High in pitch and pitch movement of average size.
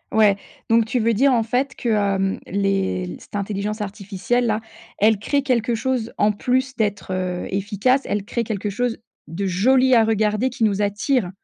Yes: high, 215 Hz; average, 3.5 semitones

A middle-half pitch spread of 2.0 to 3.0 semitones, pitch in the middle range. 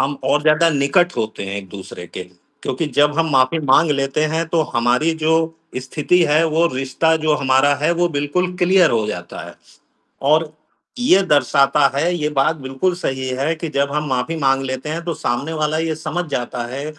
No: average, 3.5 semitones; medium, 150 Hz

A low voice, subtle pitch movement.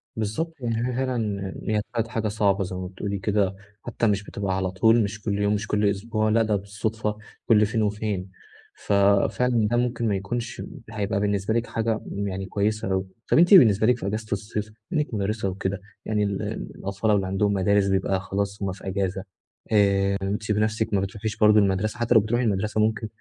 Yes: low, 105 Hz; narrow, 2.0 semitones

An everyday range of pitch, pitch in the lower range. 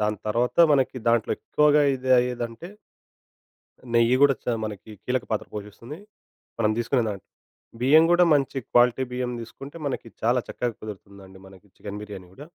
Yes: average, 3.8 semitones; low, 120 Hz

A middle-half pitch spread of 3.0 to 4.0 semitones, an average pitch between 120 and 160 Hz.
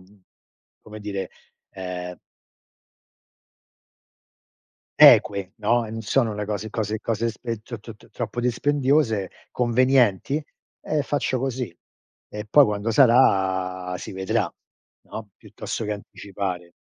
No: average, 3.7 semitones; low, 110 Hz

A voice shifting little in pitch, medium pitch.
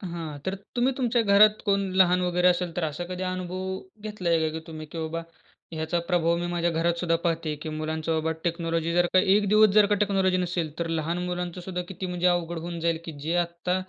Yes: narrow, 2.1 semitones; medium, 175 Hz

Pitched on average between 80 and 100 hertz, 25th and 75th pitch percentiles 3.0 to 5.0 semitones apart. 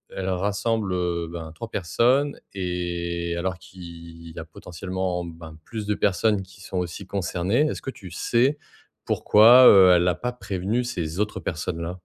Yes: very low, 95 Hz; average, 3.5 semitones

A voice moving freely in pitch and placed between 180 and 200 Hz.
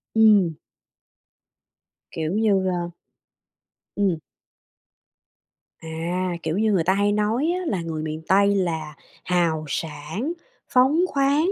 No: average, 4.9 semitones; medium, 185 Hz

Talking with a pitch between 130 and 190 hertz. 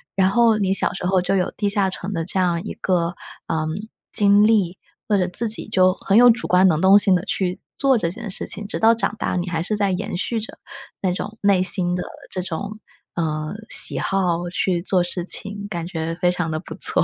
Yes: medium, 185 Hz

